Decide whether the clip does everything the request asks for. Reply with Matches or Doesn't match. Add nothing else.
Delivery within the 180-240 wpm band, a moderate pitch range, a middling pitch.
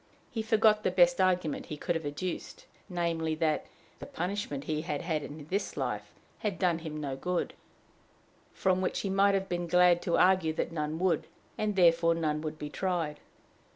Matches